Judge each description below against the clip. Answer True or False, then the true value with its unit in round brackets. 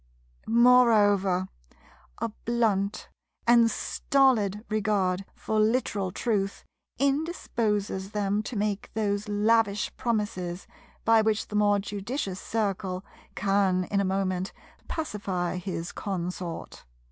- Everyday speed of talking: False (100 wpm)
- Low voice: False (205 Hz)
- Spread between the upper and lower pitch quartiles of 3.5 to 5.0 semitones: False (2.5 semitones)